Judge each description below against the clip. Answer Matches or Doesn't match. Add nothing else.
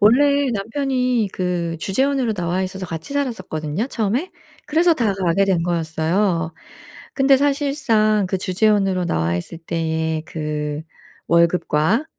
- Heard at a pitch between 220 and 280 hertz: Doesn't match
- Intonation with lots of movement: Matches